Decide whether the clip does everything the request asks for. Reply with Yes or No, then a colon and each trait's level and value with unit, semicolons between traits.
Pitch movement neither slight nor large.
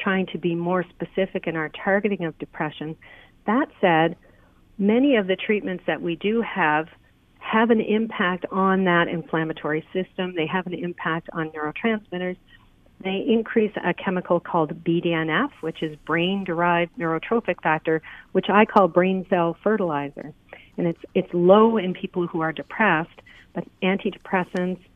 Yes: average, 3.1 semitones